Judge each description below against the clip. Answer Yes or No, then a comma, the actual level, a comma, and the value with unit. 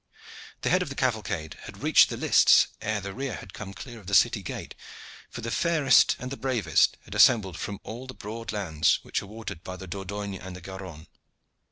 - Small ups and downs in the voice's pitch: No, average, 4.1 semitones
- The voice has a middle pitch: No, low, 105 Hz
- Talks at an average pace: No, fast, 210 wpm